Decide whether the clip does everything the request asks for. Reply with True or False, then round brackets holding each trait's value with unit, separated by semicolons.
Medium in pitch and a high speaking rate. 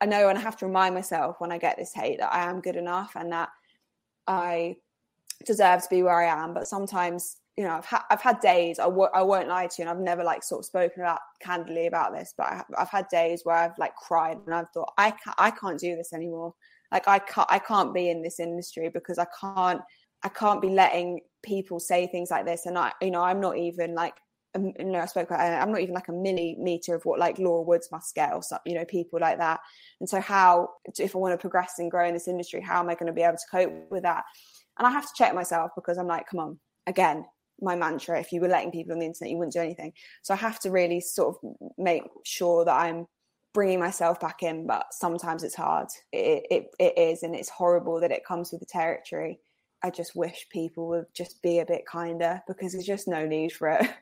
True (175 Hz; 255 wpm)